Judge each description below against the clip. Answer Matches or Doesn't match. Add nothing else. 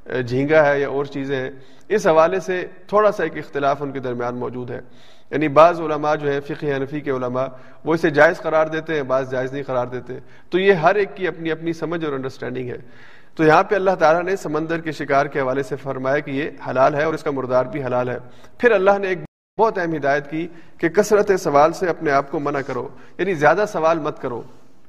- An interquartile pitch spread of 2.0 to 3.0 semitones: Doesn't match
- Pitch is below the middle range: Doesn't match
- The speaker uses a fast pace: Matches